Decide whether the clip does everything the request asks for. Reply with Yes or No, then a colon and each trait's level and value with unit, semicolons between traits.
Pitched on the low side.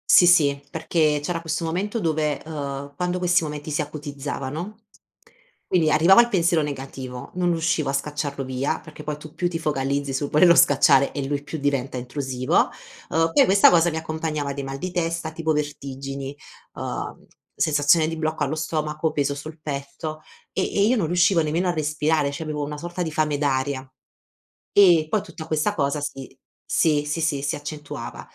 No: medium, 150 Hz